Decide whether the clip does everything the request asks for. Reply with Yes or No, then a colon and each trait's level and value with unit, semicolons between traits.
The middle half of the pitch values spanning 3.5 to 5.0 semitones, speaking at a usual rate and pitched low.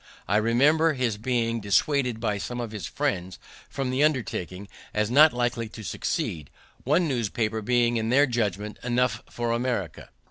No: average, 3.0 semitones; average, 155 wpm; low, 115 Hz